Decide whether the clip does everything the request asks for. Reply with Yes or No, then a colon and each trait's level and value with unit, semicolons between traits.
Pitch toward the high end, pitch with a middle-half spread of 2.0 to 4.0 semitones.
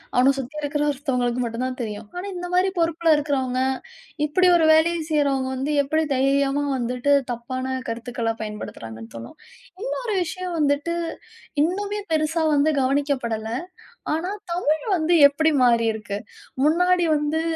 No: very high, 285 Hz; average, 4.5 semitones